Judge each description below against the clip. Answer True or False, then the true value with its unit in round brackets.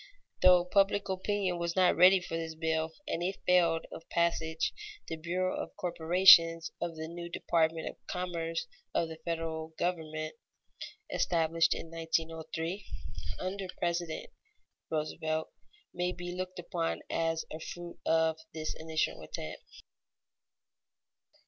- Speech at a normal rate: False (125 wpm)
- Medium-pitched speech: True (165 Hz)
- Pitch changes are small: True (1.8 semitones)